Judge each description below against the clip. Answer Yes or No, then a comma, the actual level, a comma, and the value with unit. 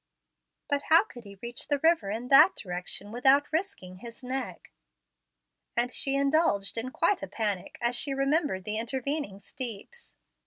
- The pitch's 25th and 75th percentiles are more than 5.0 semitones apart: Yes, wide, 5.5 semitones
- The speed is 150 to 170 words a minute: Yes, average, 155 wpm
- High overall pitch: Yes, very high, 255 Hz